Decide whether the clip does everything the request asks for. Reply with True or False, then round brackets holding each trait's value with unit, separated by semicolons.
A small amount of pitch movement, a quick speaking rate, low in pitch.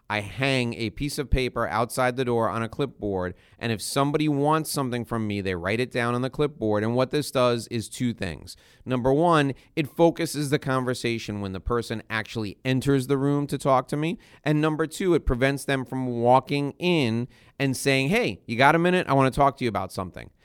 False (3.7 semitones; 215 wpm; 130 Hz)